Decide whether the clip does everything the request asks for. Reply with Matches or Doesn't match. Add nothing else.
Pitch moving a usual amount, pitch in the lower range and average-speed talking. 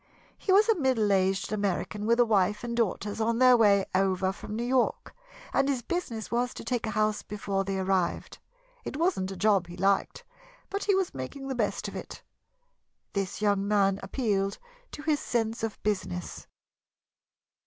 Doesn't match